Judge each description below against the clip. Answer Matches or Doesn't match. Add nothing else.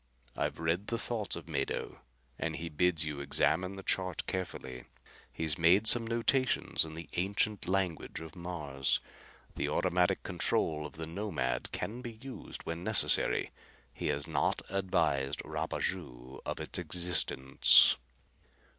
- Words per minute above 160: Doesn't match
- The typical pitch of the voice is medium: Doesn't match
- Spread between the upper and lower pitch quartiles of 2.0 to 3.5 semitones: Doesn't match